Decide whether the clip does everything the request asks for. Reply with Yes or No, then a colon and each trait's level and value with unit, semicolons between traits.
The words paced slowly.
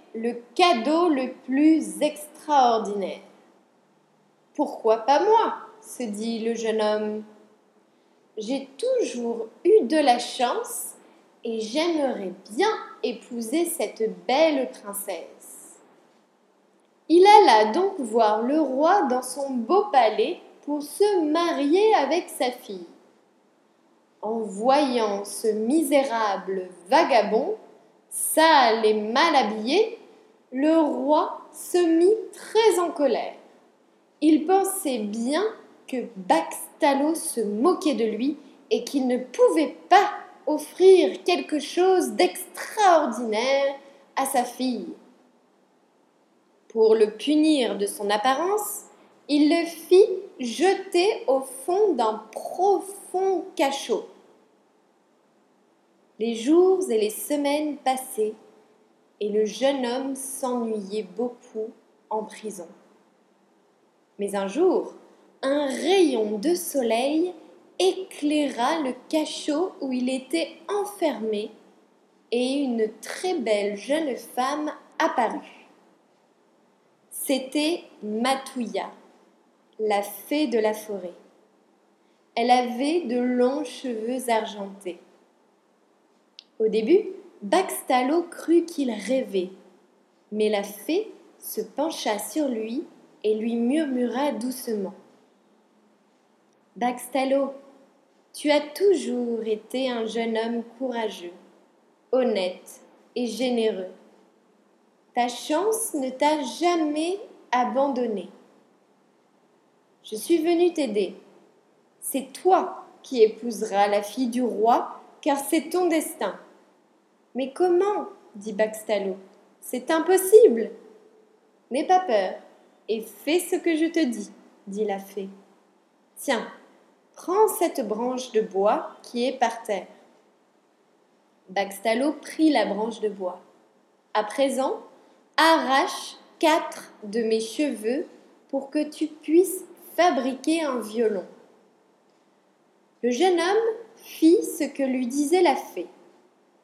Yes: slow, 105 wpm